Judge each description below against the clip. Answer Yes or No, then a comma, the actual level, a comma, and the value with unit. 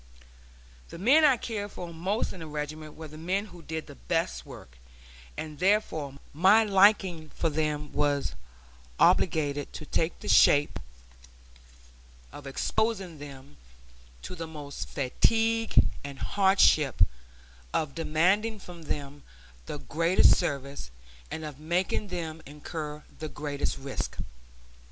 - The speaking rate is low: Yes, slow, 130 wpm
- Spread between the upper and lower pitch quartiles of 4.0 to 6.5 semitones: Yes, average, 4.4 semitones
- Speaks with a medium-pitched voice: Yes, medium, 160 Hz